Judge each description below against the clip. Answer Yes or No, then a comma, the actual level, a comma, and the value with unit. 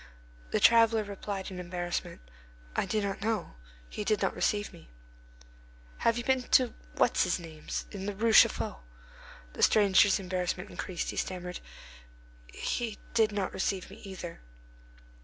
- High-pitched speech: Yes, high, 200 Hz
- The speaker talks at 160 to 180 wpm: No, average, 145 wpm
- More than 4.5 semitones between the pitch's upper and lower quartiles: No, average, 3.1 semitones